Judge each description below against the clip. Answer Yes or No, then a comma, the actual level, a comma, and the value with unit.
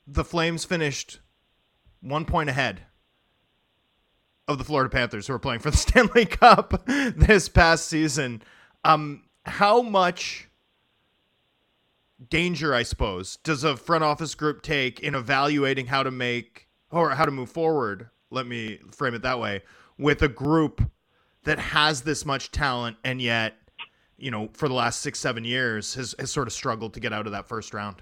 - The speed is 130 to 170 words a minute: Yes, average, 165 wpm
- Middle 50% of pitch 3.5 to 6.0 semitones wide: Yes, average, 4.8 semitones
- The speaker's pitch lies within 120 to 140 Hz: Yes, low, 135 Hz